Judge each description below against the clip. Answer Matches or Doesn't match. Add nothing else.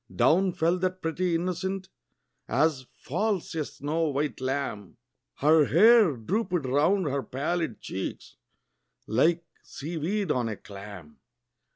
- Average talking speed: Doesn't match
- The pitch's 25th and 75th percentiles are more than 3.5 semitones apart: Matches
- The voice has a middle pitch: Matches